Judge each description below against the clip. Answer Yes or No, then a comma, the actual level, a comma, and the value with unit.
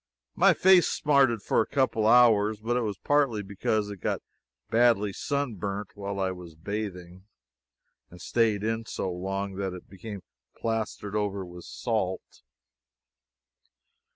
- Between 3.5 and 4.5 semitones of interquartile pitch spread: No, average, 2.9 semitones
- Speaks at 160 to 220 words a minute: No, average, 150 wpm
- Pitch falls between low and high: No, low, 105 Hz